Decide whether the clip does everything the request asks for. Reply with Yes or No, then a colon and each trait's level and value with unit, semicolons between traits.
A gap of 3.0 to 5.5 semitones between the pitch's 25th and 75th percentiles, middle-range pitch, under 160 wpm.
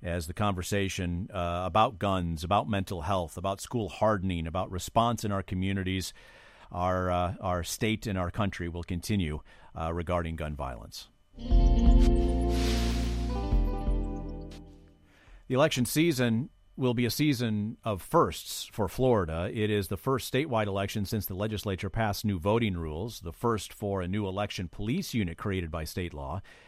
No: average, 3.9 semitones; very low, 95 Hz; average, 150 wpm